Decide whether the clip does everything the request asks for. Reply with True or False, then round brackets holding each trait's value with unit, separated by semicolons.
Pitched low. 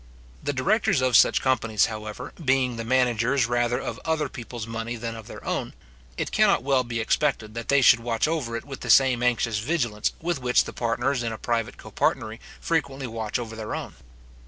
True (120 Hz)